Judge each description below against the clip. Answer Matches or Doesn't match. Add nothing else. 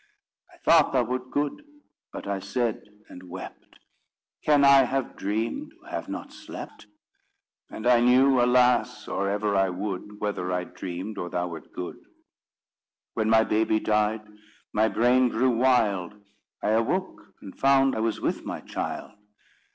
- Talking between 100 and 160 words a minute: Matches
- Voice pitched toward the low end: Matches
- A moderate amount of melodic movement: Matches